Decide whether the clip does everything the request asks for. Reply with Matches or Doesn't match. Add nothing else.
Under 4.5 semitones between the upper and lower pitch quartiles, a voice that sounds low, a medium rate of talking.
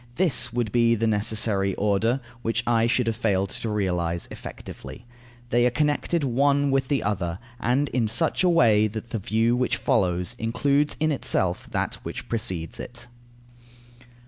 Matches